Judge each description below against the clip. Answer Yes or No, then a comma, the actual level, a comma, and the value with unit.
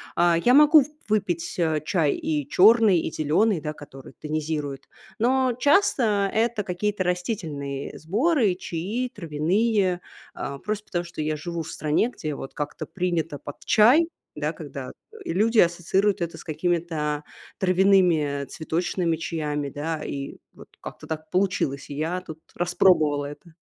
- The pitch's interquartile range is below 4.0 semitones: No, average, 5.1 semitones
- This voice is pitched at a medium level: Yes, medium, 175 Hz